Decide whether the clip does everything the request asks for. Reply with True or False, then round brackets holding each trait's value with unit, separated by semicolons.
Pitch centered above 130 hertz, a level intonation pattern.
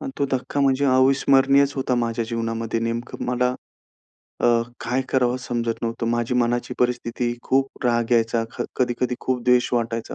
False (125 Hz; 1.8 semitones)